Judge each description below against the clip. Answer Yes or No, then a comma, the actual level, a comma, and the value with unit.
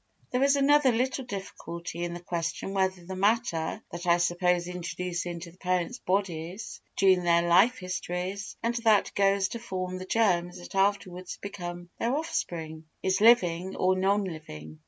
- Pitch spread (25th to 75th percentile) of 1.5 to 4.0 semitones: Yes, narrow, 2.6 semitones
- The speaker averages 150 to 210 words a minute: Yes, average, 160 wpm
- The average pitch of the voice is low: No, medium, 185 Hz